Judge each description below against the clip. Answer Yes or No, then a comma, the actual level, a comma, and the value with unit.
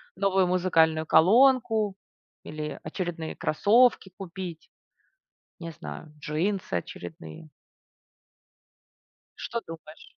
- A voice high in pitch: No, medium, 175 Hz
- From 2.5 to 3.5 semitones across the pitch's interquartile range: No, average, 4.1 semitones